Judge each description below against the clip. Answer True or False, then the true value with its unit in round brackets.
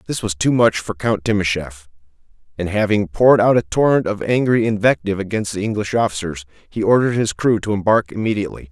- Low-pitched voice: True (105 Hz)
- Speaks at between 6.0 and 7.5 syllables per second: True (6.2 syllables/s)